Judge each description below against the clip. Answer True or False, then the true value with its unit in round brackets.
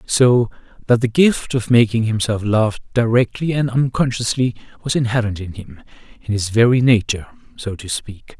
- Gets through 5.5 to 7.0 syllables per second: False (5.1 syllables/s)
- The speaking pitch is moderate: False (115 Hz)